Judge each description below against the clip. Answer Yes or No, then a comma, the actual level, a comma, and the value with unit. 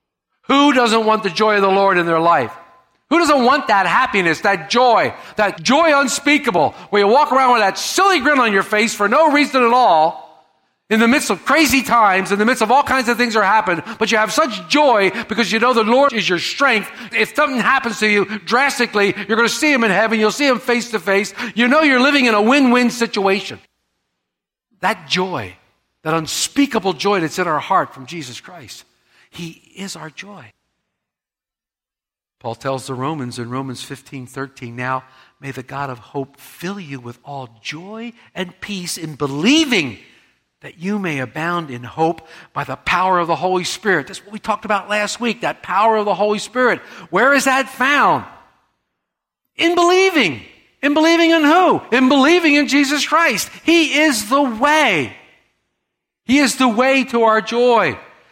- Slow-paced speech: No, average, 190 wpm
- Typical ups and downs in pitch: No, wide, 7.5 semitones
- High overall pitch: Yes, high, 215 Hz